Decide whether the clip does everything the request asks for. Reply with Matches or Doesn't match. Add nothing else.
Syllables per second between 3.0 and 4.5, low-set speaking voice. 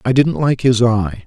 Matches